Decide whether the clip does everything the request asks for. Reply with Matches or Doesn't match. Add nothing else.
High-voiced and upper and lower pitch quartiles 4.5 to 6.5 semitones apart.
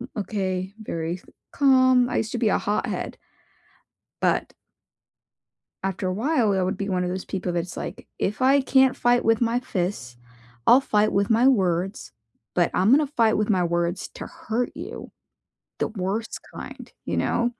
Matches